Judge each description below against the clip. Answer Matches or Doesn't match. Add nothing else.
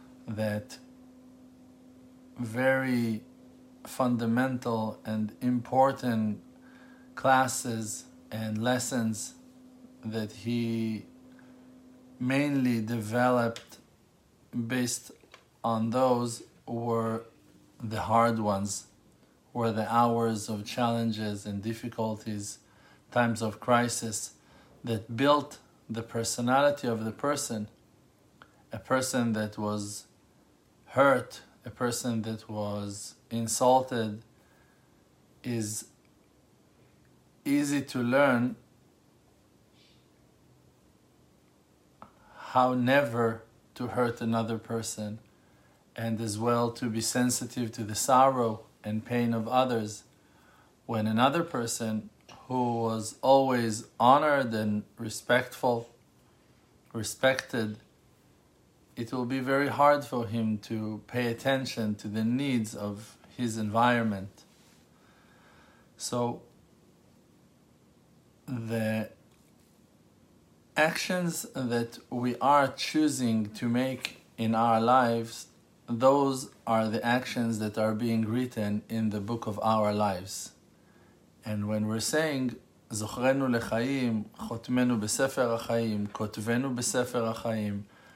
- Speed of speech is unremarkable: Doesn't match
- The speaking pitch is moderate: Doesn't match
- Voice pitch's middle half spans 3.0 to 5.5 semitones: Doesn't match